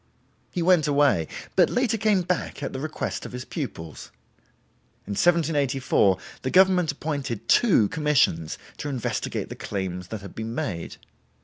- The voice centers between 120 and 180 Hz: Yes, medium, 140 Hz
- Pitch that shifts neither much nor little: No, wide, 8.5 semitones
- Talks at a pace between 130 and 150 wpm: Yes, average, 145 wpm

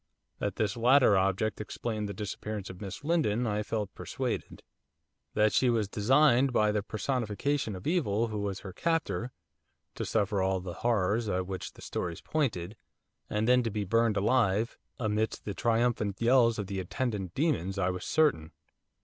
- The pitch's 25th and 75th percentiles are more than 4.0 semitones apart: No, average, 3.7 semitones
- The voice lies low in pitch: Yes, low, 105 Hz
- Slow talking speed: No, average, 165 wpm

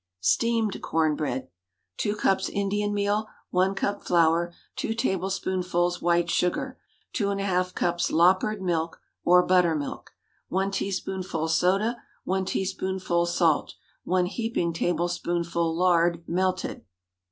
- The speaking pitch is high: No, medium, 180 Hz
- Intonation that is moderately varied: No, narrow, 2.3 semitones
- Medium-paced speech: No, slow, 110 wpm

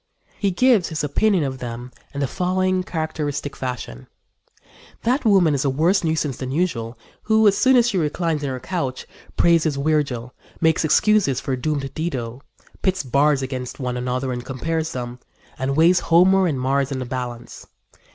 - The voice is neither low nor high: Yes, medium, 145 Hz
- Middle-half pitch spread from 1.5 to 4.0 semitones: No, wide, 5.5 semitones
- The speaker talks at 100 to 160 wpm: No, average, 170 wpm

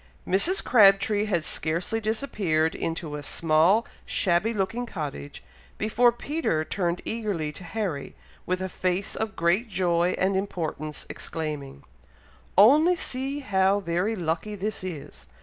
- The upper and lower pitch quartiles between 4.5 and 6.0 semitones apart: Yes, average, 4.8 semitones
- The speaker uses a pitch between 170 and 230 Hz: Yes, high, 190 Hz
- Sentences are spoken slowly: Yes, slow, 130 wpm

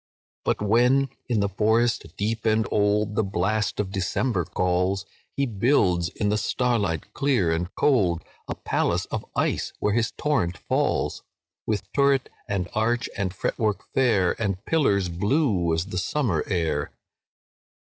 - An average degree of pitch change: Yes, average, 4.5 semitones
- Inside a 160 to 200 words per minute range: No, average, 145 wpm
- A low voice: Yes, low, 105 Hz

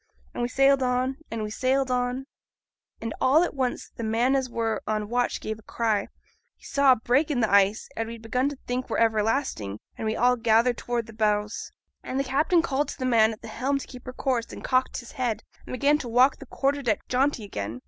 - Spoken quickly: Yes, fast, 230 wpm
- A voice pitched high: Yes, high, 245 Hz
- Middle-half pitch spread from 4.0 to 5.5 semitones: No, average, 3.2 semitones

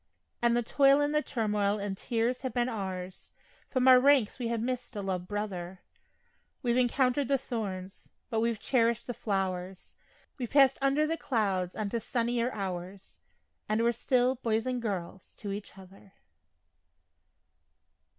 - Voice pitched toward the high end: Yes, high, 230 Hz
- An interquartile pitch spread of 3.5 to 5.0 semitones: Yes, average, 4.3 semitones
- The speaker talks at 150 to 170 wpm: Yes, average, 155 wpm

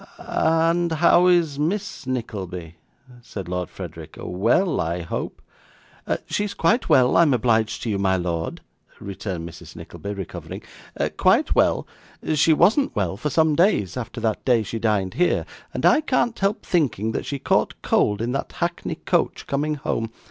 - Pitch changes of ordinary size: No, wide, 9.0 semitones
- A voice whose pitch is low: Yes, low, 125 Hz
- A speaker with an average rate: Yes, average, 165 wpm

